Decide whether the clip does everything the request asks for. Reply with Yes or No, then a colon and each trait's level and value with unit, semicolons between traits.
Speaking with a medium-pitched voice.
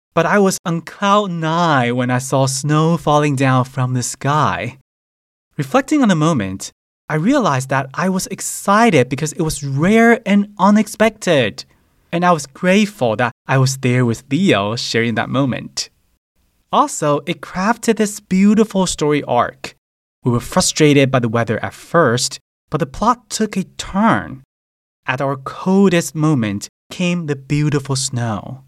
Yes: medium, 150 Hz